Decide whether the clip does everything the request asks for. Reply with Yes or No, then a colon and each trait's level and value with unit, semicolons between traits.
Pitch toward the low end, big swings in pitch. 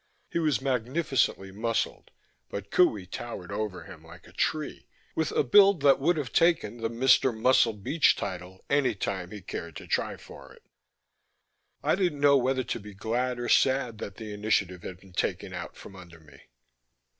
Yes: low, 115 Hz; wide, 5.8 semitones